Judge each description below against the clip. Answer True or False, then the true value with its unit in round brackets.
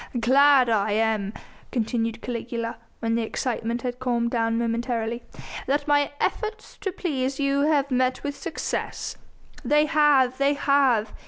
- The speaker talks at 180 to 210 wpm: False (140 wpm)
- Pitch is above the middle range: True (255 Hz)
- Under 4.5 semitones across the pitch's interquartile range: True (3.6 semitones)